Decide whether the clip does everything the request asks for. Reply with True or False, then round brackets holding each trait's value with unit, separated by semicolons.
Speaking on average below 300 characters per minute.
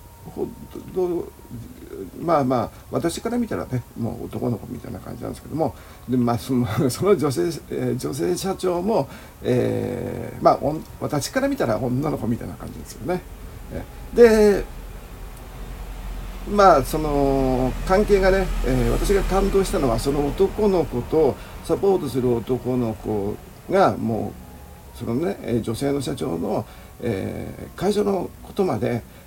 True (250 characters per minute)